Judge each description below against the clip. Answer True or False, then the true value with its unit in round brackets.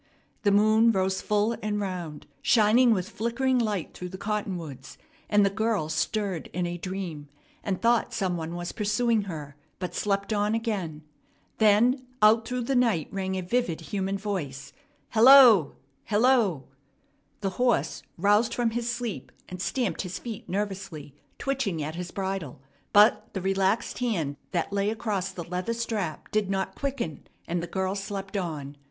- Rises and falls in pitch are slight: False (4.0 semitones)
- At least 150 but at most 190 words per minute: True (160 wpm)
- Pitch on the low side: False (200 Hz)